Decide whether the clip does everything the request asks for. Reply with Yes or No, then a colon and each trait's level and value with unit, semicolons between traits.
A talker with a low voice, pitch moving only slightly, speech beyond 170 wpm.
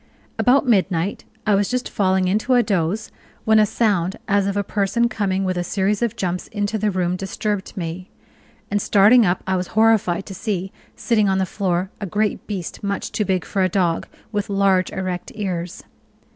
No: high, 195 Hz; narrow, 2.3 semitones; average, 190 wpm